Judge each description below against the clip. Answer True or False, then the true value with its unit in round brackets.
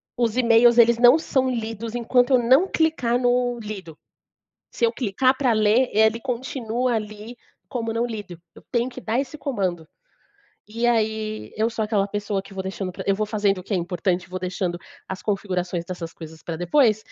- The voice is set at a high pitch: True (220 Hz)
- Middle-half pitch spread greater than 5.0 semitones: False (3.8 semitones)